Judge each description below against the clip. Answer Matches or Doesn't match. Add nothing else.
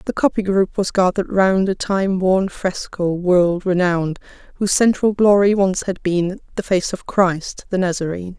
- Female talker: Matches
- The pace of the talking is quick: Doesn't match